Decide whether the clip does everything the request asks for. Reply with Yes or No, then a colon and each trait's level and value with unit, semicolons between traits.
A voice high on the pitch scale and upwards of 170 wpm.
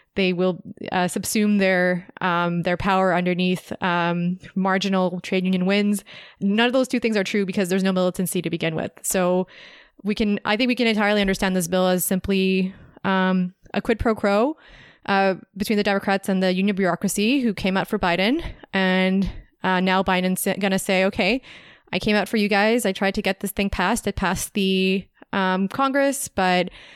Yes: high, 195 Hz; average, 190 wpm